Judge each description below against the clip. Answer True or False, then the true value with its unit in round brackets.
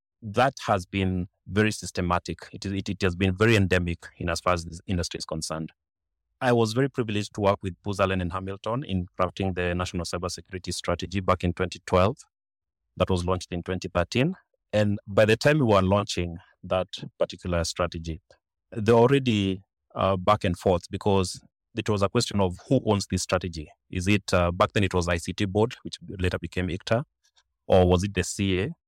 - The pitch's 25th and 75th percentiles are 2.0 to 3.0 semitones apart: True (2.7 semitones)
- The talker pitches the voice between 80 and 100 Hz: True (95 Hz)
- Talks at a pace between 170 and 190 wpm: True (185 wpm)